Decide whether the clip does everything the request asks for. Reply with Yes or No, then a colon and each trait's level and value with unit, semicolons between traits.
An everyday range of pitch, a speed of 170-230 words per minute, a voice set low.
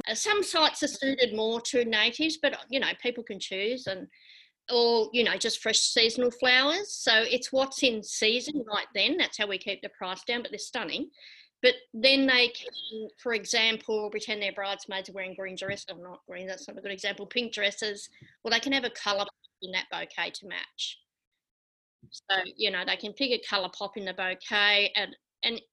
No: average, 4.0 semitones; average, 200 wpm; high, 220 Hz